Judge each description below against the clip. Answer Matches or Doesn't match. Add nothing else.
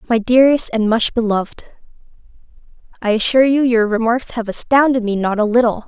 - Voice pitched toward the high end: Matches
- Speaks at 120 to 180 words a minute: Matches